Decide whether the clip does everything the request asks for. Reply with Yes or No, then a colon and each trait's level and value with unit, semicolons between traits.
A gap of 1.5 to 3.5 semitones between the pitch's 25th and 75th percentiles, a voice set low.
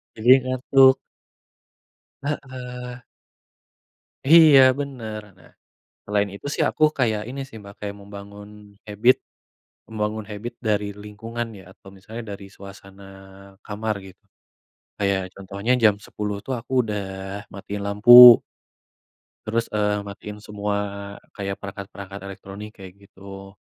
Yes: average, 2.8 semitones; low, 105 Hz